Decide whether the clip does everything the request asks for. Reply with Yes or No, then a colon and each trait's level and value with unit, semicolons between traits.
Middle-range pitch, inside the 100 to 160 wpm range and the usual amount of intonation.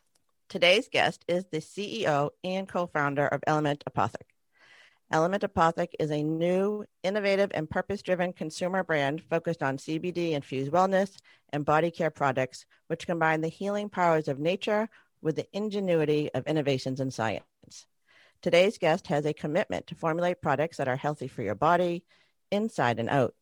Yes: medium, 160 Hz; average, 150 wpm; average, 3.8 semitones